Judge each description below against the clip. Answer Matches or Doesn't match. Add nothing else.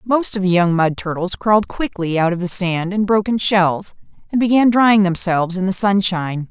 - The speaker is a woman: Matches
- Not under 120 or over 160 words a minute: Doesn't match